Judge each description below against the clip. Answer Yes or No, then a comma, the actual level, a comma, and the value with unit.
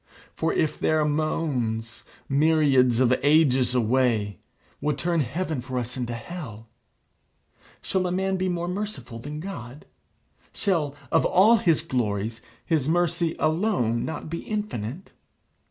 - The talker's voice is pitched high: No, medium, 150 Hz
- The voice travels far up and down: Yes, wide, 5.7 semitones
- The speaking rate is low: Yes, slow, 130 wpm